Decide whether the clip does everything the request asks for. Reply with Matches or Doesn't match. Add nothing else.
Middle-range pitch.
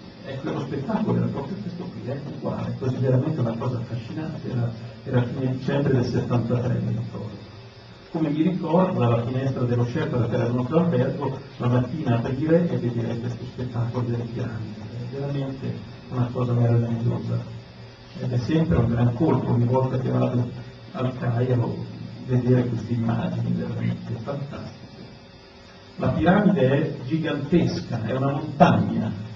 Doesn't match